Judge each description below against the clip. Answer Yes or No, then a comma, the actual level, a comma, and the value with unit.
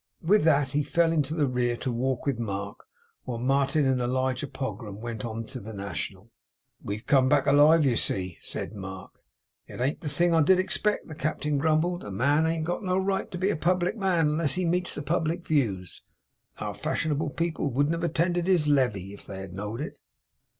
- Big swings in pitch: Yes, wide, 5.8 semitones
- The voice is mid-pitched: Yes, medium, 145 Hz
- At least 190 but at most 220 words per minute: Yes, fast, 205 wpm